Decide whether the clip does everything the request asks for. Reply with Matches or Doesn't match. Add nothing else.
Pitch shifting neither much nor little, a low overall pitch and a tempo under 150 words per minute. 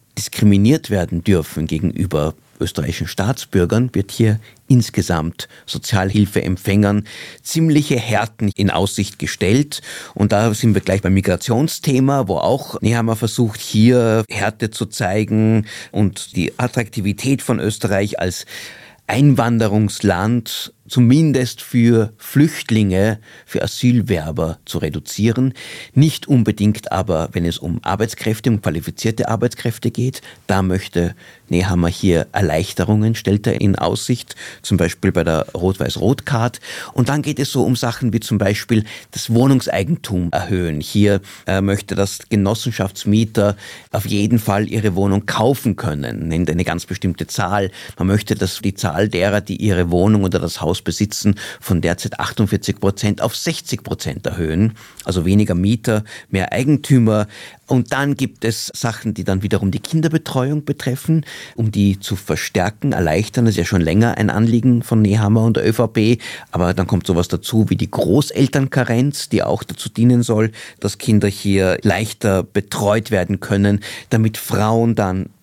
Matches